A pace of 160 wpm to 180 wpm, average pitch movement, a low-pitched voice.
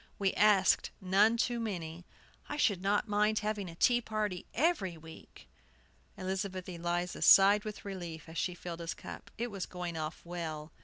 No: average, 165 wpm; average, 3.4 semitones; high, 190 Hz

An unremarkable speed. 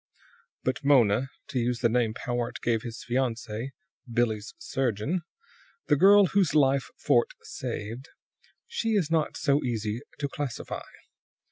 No: slow, 130 wpm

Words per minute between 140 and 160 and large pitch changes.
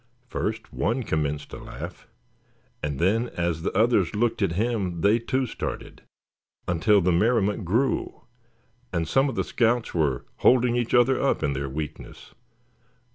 Yes: average, 150 wpm; wide, 6.2 semitones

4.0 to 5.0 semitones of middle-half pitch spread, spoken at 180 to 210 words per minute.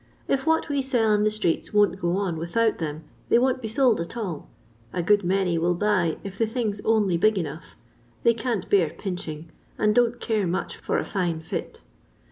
Yes: average, 4.7 semitones; average, 200 wpm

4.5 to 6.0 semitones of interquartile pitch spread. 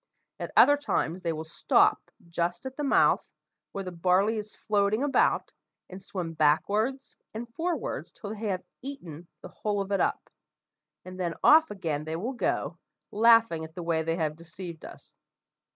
Yes: average, 5.2 semitones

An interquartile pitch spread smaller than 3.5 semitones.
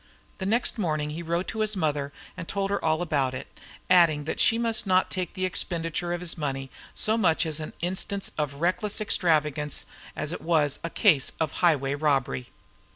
No: average, 3.9 semitones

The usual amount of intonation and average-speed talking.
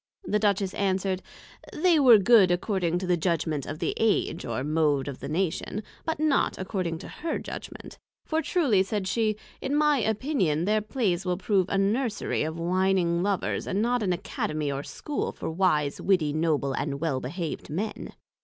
Yes: average, 5.0 semitones; average, 175 wpm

